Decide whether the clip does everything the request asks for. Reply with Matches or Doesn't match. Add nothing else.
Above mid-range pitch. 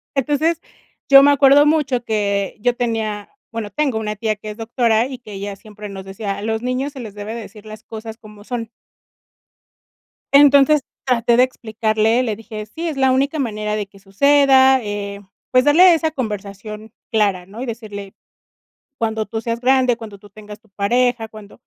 Matches